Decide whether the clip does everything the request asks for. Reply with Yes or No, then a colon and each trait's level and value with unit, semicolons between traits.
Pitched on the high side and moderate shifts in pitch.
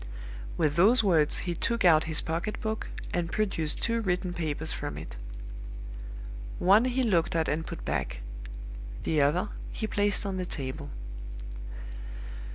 No: medium, 175 Hz; average, 4.9 semitones